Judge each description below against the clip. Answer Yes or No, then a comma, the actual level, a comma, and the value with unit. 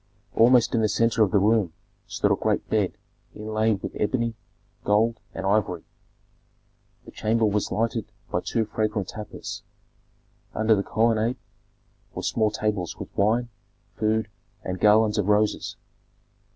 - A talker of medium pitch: No, low, 110 Hz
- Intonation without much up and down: Yes, narrow, 1.5 semitones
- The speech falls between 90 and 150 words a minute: Yes, average, 140 wpm